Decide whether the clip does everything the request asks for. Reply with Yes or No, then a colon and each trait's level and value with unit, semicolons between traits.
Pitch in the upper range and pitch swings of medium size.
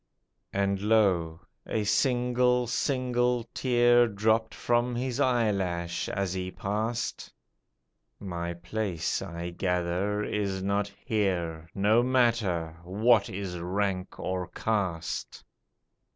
No: low, 100 Hz; average, 4.8 semitones